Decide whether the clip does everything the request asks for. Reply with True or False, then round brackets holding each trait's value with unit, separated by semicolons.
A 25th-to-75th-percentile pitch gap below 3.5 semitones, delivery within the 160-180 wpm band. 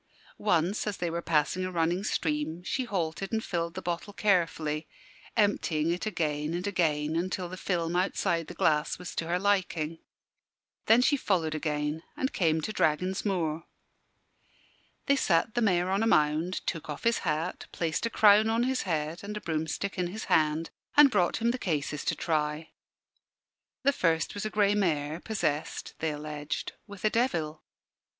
False (4.4 semitones; 170 wpm)